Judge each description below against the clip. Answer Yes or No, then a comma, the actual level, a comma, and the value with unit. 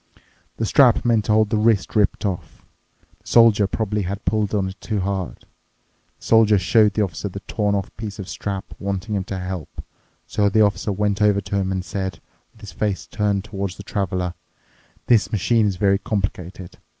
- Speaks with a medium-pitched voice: No, low, 100 Hz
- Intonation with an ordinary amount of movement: No, narrow, 1.9 semitones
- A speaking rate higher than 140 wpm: Yes, average, 190 wpm